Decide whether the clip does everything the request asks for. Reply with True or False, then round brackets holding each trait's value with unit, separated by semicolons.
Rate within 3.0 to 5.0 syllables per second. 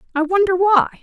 False (5.5 syllables/s)